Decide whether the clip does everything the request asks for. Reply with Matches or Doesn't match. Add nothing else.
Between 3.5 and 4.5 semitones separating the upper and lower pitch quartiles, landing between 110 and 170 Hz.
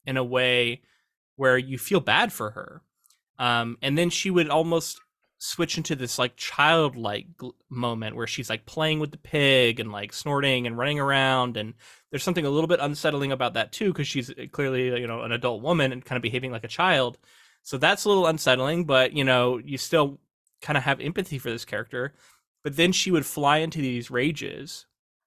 Matches